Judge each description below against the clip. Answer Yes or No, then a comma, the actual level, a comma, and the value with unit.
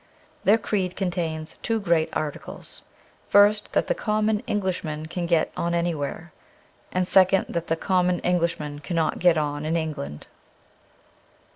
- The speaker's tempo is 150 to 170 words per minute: No, average, 140 wpm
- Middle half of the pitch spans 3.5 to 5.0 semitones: No, average, 3.1 semitones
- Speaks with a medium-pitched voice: Yes, medium, 170 Hz